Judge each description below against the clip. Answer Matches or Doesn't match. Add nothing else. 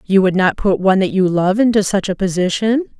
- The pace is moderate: Doesn't match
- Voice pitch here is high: Matches